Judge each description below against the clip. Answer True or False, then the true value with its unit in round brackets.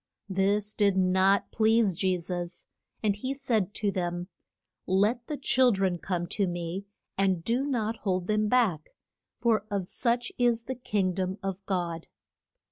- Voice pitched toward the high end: True (200 Hz)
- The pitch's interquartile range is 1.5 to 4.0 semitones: True (3.6 semitones)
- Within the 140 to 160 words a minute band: True (155 wpm)